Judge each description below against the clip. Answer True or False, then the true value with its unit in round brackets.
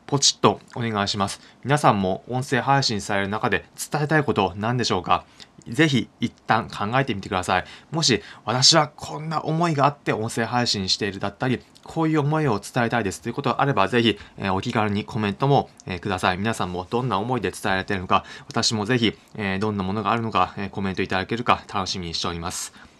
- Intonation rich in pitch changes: False (4.9 semitones)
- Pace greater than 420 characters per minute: True (430 characters per minute)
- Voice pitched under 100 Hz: False (110 Hz)